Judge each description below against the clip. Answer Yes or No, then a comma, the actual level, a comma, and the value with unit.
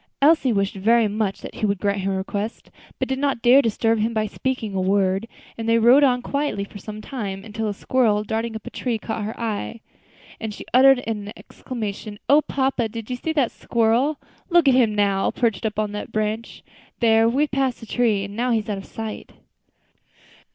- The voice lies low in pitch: No, high, 225 Hz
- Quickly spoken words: Yes, fast, 215 wpm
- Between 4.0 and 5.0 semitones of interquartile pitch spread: No, average, 3.2 semitones